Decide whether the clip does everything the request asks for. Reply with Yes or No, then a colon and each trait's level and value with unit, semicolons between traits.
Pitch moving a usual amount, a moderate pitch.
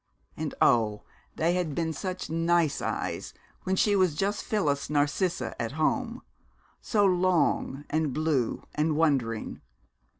Yes: average, 4.3 semitones; medium, 160 Hz